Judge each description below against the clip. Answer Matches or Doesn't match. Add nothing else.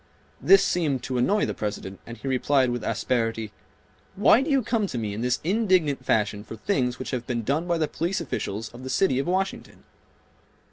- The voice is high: Doesn't match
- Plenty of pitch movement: Matches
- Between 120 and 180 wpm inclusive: Doesn't match